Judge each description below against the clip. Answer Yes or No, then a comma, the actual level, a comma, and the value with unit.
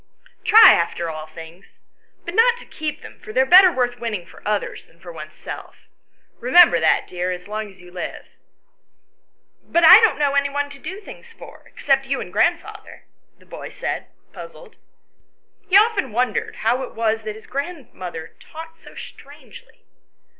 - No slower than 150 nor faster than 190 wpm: Yes, average, 170 wpm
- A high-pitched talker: Yes, very high, 255 Hz